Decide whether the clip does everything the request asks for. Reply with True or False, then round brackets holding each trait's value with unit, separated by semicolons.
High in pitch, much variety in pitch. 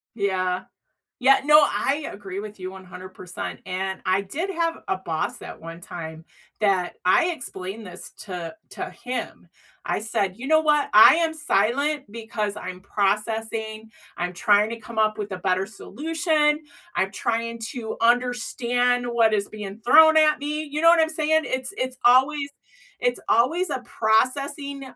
True (230 Hz; 6.8 semitones)